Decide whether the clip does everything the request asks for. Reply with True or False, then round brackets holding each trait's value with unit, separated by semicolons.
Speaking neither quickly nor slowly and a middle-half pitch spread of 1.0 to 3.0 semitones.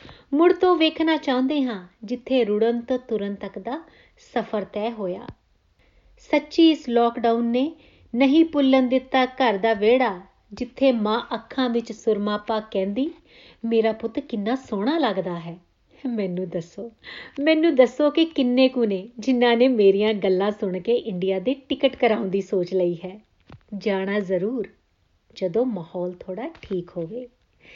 False (140 wpm; 4.5 semitones)